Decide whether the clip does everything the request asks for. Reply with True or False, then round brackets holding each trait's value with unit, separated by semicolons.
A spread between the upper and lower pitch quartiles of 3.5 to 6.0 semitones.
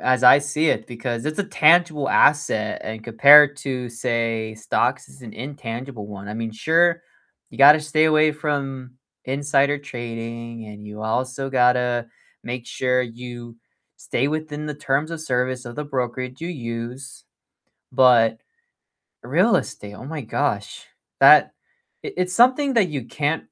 True (4.2 semitones)